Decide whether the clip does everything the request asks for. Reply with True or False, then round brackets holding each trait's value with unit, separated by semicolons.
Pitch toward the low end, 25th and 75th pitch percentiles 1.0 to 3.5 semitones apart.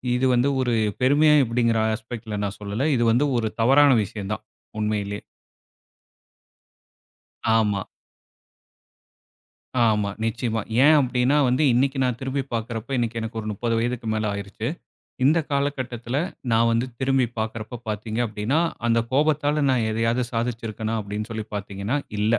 True (115 Hz; 3.0 semitones)